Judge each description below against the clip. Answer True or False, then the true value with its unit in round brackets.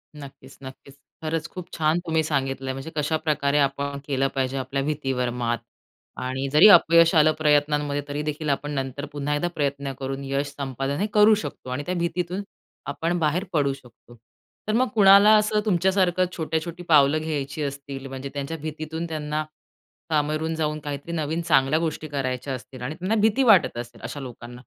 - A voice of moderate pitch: True (150 Hz)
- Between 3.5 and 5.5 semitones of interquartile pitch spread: False (3.1 semitones)